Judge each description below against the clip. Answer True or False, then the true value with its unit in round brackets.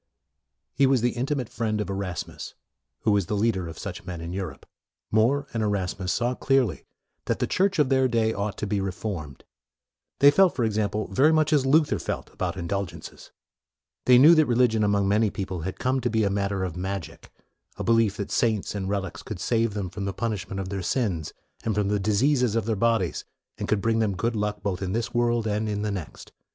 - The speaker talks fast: True (215 wpm)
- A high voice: False (105 Hz)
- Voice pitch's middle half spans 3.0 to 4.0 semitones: True (3.5 semitones)